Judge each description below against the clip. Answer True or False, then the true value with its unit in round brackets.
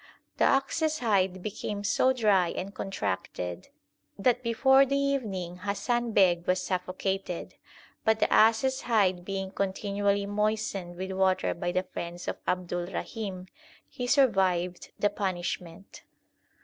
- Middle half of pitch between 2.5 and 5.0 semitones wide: True (3.5 semitones)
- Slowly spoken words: True (130 wpm)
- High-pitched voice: True (195 Hz)